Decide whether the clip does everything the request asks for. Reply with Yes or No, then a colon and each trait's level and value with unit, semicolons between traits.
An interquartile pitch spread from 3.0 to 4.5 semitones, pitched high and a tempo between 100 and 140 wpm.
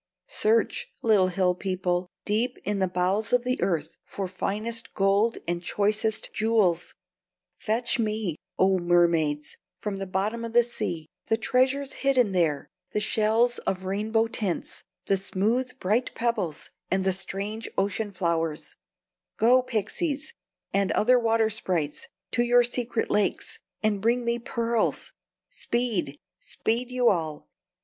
Yes: average, 4.1 semitones; high, 215 Hz; slow, 135 wpm